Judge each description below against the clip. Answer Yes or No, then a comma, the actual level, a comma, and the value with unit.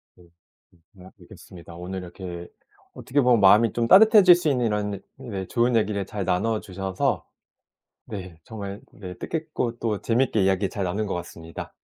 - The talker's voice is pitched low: Yes, low, 105 Hz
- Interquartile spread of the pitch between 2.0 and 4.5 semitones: Yes, average, 4.2 semitones